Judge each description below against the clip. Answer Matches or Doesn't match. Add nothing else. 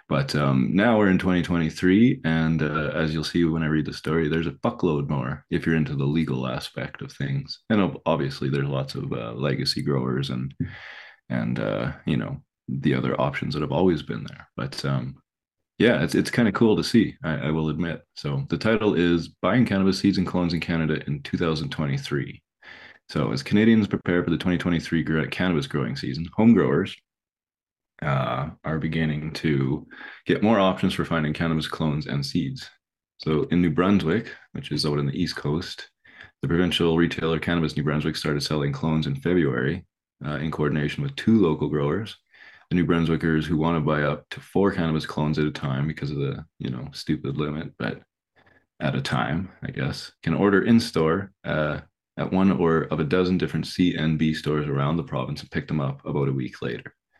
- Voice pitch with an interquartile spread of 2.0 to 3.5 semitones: Matches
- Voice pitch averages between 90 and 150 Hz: Doesn't match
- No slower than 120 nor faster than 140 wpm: Doesn't match